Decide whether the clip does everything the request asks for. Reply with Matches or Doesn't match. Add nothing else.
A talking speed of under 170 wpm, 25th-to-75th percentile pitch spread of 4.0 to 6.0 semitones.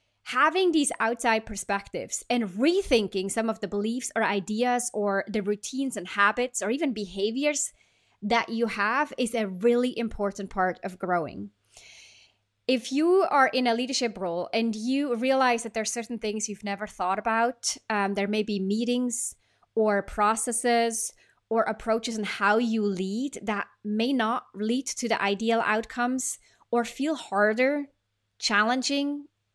Doesn't match